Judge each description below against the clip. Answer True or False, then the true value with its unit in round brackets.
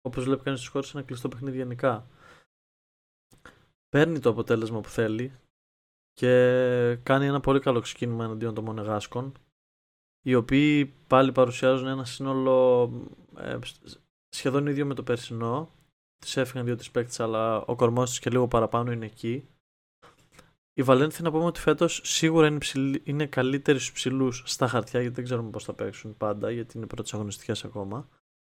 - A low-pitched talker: True (125 Hz)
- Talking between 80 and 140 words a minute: False (150 wpm)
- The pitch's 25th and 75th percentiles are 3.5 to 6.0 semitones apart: False (3.0 semitones)